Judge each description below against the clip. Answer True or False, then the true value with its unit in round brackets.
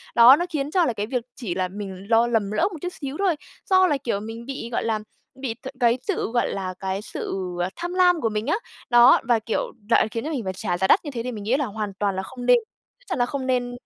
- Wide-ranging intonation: False (4.7 semitones)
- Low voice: False (235 Hz)